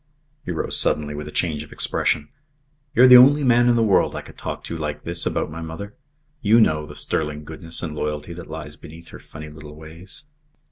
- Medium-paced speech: No, fast, 215 wpm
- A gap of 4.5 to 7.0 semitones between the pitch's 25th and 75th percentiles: No, average, 3.9 semitones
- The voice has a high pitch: No, very low, 80 Hz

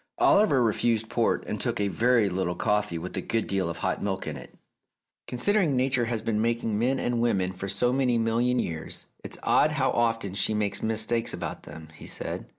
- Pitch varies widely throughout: No, average, 3.7 semitones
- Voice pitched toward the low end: Yes, low, 115 Hz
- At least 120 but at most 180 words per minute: No, average, 200 wpm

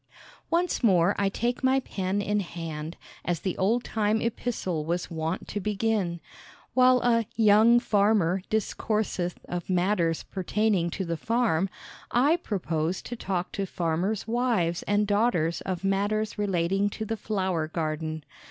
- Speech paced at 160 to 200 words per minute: No, average, 145 wpm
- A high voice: Yes, high, 195 Hz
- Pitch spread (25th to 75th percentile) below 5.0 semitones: Yes, average, 4.2 semitones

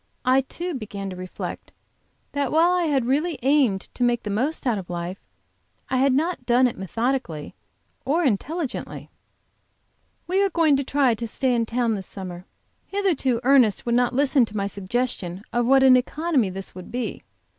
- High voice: Yes, very high, 250 Hz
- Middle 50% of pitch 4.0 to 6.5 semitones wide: Yes, wide, 5.4 semitones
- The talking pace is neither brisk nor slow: Yes, average, 175 wpm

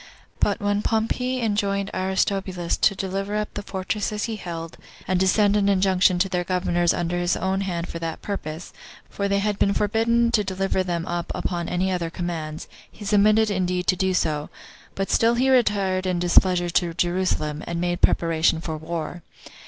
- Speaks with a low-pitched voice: No, medium, 185 Hz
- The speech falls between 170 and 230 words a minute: Yes, average, 180 wpm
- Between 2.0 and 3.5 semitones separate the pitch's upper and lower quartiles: Yes, average, 2.7 semitones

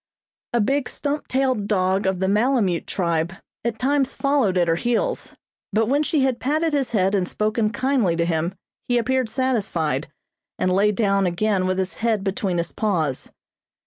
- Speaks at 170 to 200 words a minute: Yes, average, 175 wpm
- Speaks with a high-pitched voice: Yes, high, 210 Hz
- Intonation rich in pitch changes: Yes, wide, 5.7 semitones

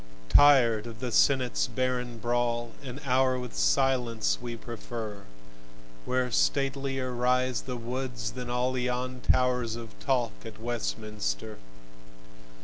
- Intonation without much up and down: Yes, narrow, 1.7 semitones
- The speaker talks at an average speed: No, slow, 120 wpm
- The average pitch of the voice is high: No, low, 125 Hz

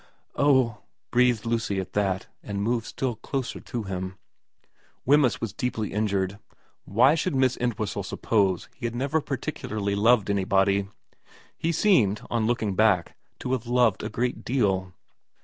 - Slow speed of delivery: No, average, 150 wpm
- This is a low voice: Yes, low, 110 Hz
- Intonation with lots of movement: No, average, 3.9 semitones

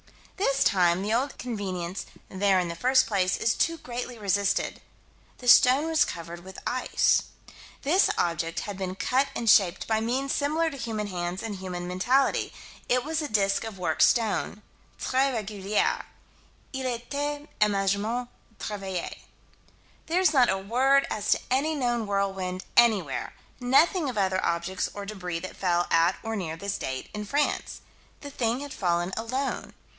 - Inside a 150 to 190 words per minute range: Yes, average, 160 wpm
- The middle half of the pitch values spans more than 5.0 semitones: Yes, wide, 5.6 semitones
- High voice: Yes, high, 215 Hz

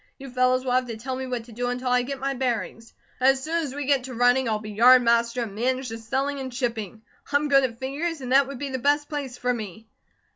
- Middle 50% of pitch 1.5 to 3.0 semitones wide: Yes, narrow, 2.5 semitones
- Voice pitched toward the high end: Yes, very high, 255 Hz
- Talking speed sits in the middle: No, fast, 260 wpm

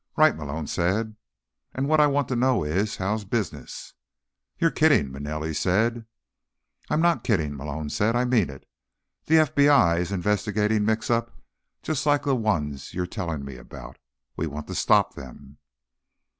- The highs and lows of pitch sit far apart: Yes, wide, 8.2 semitones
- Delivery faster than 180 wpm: No, average, 155 wpm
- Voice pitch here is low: Yes, low, 105 Hz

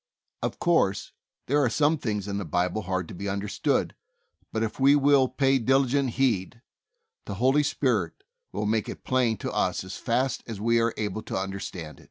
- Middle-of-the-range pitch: No, low, 115 Hz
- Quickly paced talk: No, average, 190 wpm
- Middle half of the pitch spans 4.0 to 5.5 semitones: Yes, average, 5.2 semitones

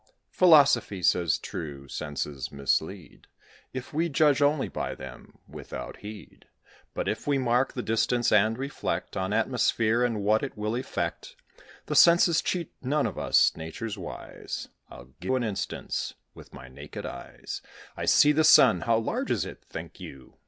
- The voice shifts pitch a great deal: Yes, wide, 7.4 semitones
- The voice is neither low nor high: No, low, 115 Hz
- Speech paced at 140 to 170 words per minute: Yes, average, 160 wpm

